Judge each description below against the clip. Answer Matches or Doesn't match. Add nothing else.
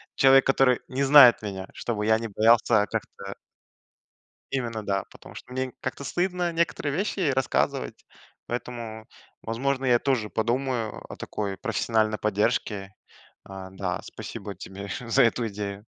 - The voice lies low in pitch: Matches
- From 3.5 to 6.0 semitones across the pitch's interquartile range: Matches